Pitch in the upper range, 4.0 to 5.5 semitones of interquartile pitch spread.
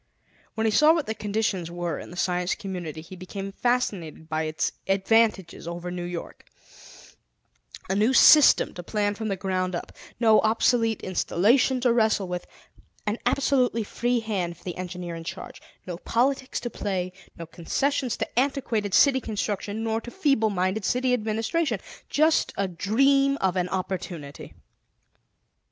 Yes: high, 205 Hz; average, 5.0 semitones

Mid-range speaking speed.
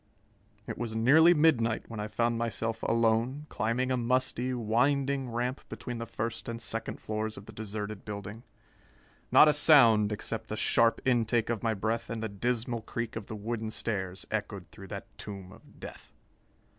Yes: average, 170 wpm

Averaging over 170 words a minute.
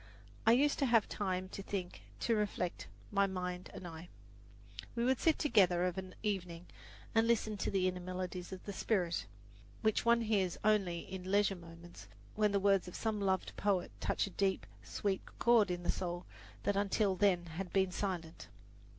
Yes: average, 180 wpm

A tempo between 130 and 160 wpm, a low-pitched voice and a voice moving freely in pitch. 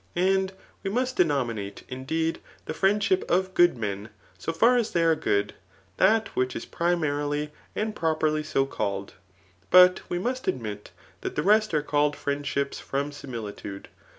No: average, 155 wpm; medium, 155 Hz; wide, 6.2 semitones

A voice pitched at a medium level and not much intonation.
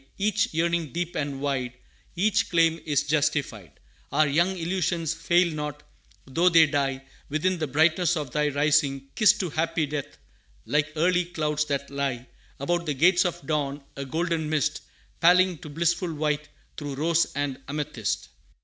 No: medium, 155 Hz; average, 3.1 semitones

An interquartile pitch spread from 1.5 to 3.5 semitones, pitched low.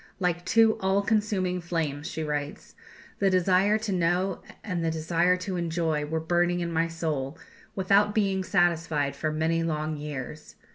No: average, 3.1 semitones; medium, 170 Hz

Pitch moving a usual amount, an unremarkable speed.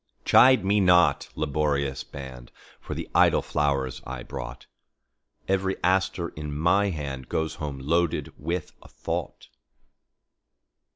No: average, 4.8 semitones; slow, 105 wpm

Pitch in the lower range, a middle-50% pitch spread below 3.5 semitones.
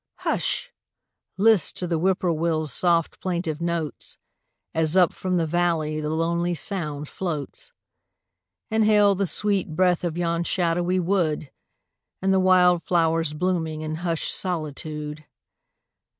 No: medium, 170 Hz; narrow, 2.6 semitones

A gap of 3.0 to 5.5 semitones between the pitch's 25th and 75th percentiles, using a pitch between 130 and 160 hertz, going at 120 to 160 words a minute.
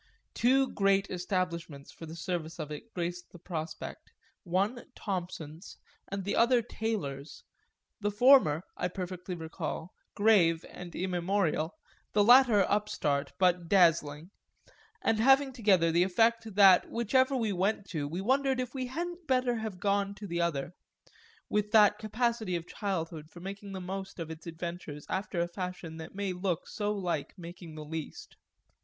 No: average, 4.0 semitones; medium, 185 Hz; average, 155 wpm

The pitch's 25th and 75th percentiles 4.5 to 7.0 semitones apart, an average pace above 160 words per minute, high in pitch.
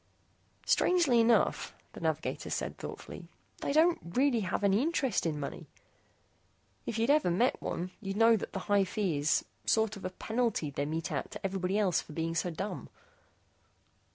Yes: average, 5.1 semitones; average, 170 wpm; high, 200 Hz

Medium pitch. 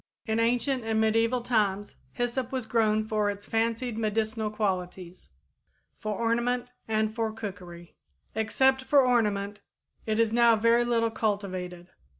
No: high, 220 Hz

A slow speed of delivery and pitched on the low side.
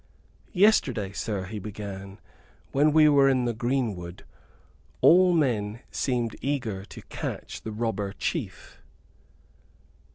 Yes: slow, 110 wpm; low, 115 Hz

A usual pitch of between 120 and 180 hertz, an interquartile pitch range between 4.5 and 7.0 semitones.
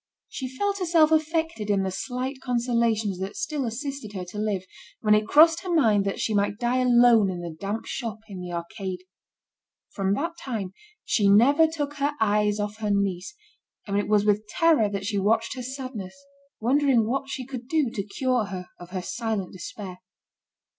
No: high, 220 Hz; average, 5.2 semitones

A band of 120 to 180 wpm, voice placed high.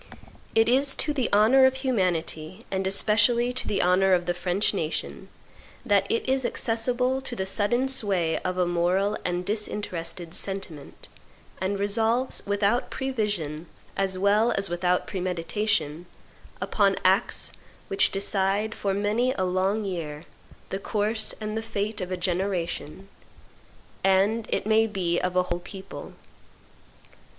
Yes: average, 140 wpm; high, 195 Hz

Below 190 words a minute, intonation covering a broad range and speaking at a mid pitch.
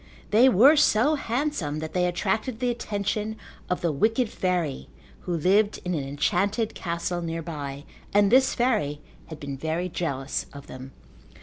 Yes: average, 150 wpm; wide, 6.2 semitones; medium, 180 Hz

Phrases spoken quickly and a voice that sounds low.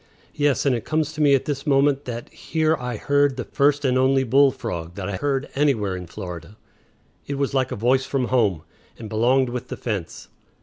Yes: fast, 210 wpm; low, 130 Hz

